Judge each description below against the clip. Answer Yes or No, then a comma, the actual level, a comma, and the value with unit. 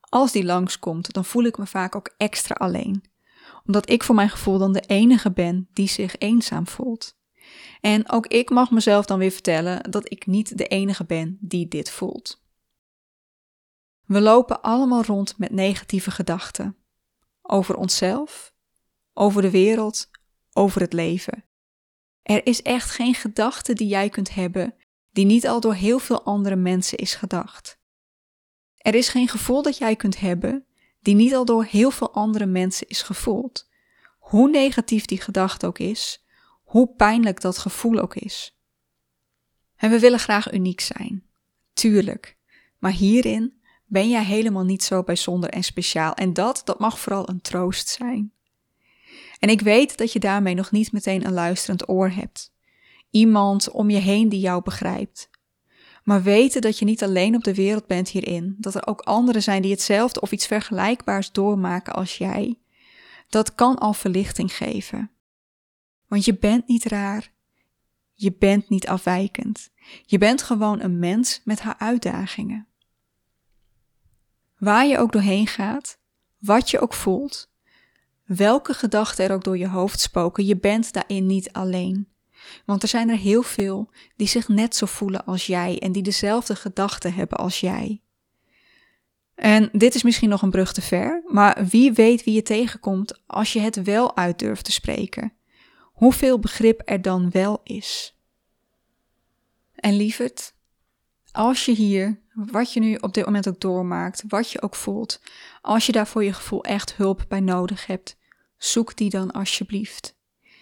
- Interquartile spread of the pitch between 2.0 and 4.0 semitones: Yes, average, 3.0 semitones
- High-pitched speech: Yes, high, 205 Hz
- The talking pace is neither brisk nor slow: Yes, average, 160 wpm